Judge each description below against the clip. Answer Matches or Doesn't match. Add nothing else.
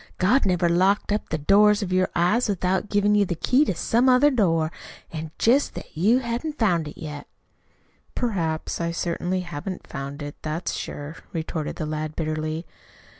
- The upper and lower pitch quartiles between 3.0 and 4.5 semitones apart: Doesn't match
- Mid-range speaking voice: Matches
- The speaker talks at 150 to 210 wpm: Matches